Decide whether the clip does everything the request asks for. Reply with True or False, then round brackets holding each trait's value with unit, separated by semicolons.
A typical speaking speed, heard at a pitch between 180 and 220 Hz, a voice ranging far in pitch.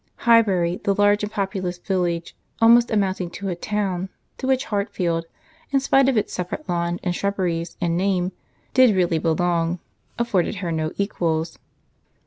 False (150 wpm; 185 Hz; 3.2 semitones)